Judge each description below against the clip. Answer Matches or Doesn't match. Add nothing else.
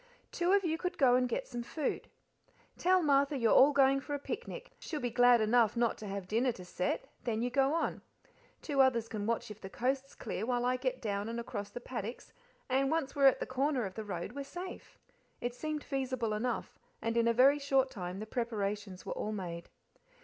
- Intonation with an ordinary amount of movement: Matches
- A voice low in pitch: Doesn't match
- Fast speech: Matches